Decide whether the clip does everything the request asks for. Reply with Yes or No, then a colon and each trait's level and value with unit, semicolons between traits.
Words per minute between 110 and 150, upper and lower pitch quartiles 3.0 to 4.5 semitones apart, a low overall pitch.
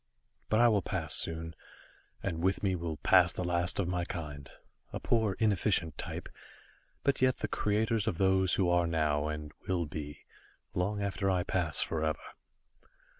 No: average, 165 wpm; average, 3.5 semitones; very low, 90 Hz